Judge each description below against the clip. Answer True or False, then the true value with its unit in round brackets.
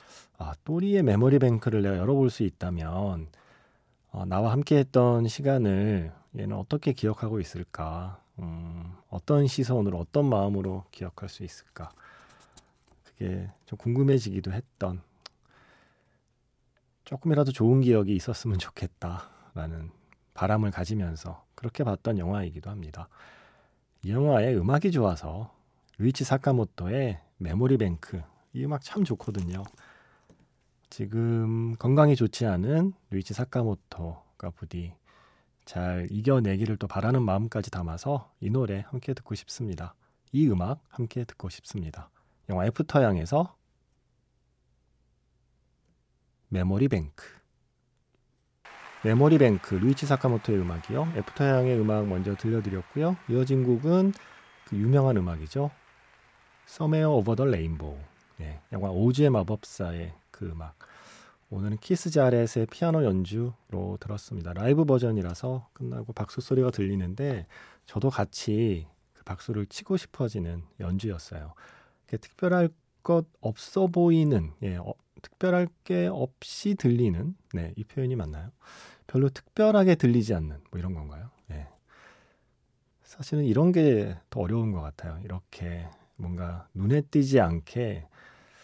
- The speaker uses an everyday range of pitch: False (6.6 semitones)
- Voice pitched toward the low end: True (110 Hz)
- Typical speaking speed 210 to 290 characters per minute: True (275 characters per minute)